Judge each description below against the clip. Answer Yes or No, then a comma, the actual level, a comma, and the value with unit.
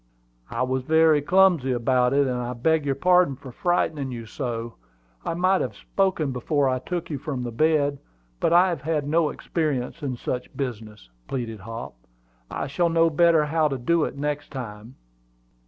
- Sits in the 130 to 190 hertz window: Yes, medium, 140 Hz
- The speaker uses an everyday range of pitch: Yes, average, 4.4 semitones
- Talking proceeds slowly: No, average, 180 wpm